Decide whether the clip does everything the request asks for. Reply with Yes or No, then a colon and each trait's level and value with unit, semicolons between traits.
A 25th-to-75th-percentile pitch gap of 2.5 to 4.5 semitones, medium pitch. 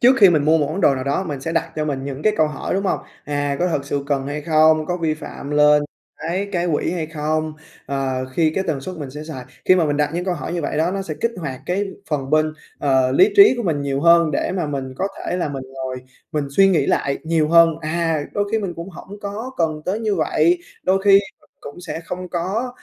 Yes: average, 3.8 semitones; medium, 160 Hz